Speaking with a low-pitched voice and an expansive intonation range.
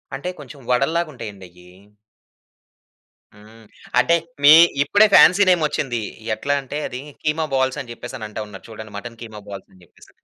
Yes: low, 125 Hz; wide, 5.7 semitones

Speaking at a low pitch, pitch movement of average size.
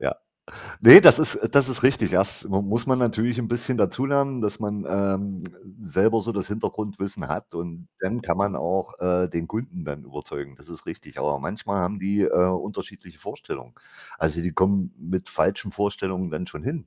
Yes: low, 100 Hz; average, 3.9 semitones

